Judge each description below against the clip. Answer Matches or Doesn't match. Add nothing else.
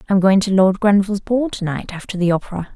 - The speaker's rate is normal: Doesn't match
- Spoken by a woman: Matches